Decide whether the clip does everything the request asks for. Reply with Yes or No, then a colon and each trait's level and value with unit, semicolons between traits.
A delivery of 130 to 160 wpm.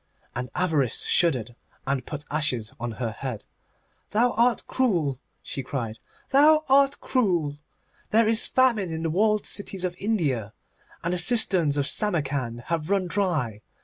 Yes: average, 145 wpm